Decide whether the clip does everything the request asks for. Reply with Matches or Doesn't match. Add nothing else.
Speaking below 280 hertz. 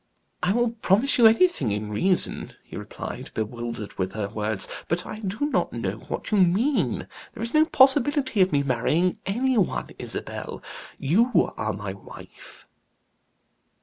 Matches